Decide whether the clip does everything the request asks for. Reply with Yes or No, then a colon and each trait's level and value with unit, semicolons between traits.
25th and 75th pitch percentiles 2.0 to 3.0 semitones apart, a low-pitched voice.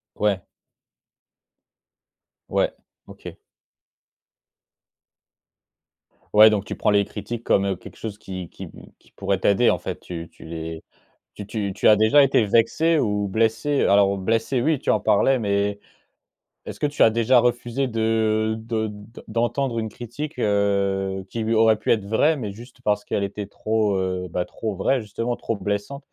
Yes: average, 2.7 semitones; low, 110 Hz